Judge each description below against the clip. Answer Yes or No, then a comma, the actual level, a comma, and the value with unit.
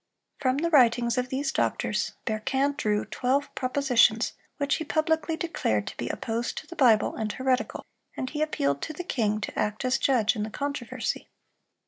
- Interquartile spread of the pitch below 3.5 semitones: No, average, 4.5 semitones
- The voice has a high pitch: Yes, very high, 255 Hz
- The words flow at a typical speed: Yes, average, 175 wpm